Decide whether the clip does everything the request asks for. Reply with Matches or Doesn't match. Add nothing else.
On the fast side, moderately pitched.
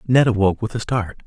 Doesn't match